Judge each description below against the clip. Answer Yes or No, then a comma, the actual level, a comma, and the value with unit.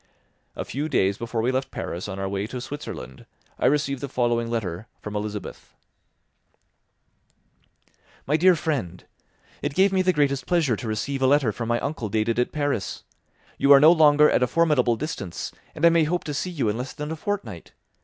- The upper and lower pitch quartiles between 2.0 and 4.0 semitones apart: No, average, 5.3 semitones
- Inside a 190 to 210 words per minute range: Yes, average, 195 wpm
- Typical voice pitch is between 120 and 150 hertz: Yes, low, 135 Hz